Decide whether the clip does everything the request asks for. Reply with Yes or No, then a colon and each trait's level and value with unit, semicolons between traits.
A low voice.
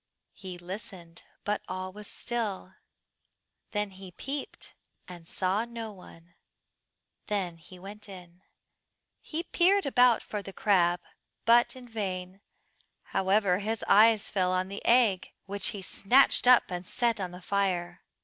No: high, 195 Hz